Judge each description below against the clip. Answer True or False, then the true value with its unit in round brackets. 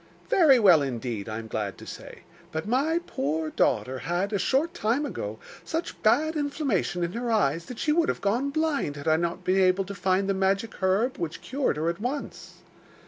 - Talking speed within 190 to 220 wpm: True (200 wpm)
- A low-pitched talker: False (195 Hz)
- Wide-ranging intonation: True (8.9 semitones)